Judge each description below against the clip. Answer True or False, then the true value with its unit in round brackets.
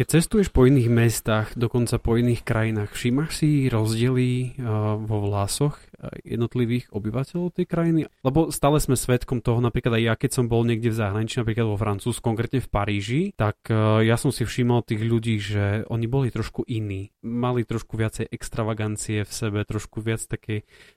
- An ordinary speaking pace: False (170 wpm)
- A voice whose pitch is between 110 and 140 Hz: True (115 Hz)